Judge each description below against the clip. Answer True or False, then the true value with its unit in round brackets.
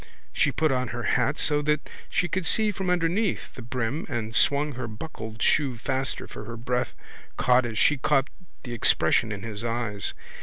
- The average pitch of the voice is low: True (130 Hz)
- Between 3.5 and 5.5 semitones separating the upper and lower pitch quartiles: True (4.7 semitones)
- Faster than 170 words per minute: True (185 wpm)